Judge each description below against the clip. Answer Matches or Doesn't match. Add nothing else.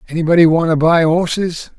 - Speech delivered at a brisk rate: Doesn't match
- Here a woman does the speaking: Doesn't match